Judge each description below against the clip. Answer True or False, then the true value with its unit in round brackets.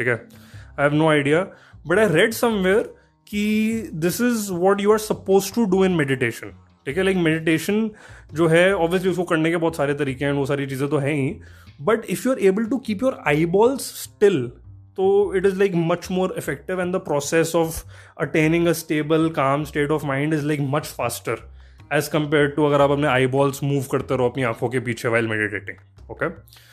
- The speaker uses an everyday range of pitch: False (5.7 semitones)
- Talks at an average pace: False (200 wpm)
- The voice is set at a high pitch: False (155 Hz)